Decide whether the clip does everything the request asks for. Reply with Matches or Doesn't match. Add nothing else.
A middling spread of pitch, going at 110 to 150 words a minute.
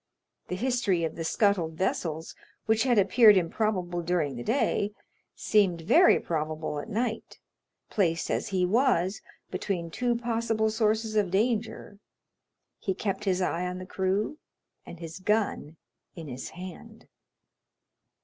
Matches